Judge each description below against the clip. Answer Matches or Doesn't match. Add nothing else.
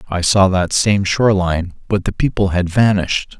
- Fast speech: Doesn't match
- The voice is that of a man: Matches